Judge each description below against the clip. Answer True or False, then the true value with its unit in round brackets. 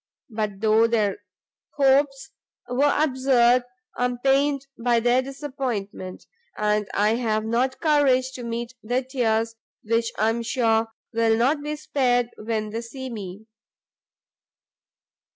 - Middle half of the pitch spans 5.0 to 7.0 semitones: False (3.0 semitones)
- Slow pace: True (130 wpm)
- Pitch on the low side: False (240 Hz)